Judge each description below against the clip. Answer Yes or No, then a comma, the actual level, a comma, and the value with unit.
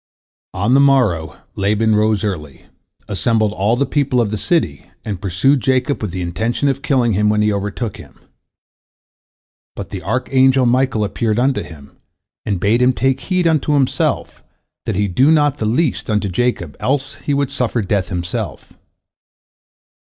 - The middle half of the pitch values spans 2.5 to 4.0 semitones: No, average, 4.9 semitones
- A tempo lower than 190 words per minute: Yes, average, 160 wpm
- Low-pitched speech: Yes, low, 115 Hz